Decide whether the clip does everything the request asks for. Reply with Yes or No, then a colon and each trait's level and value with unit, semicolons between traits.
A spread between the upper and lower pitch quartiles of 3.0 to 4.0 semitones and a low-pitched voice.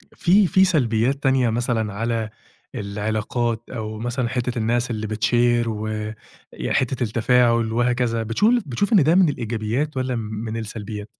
No: narrow, 2.5 semitones; low, 120 Hz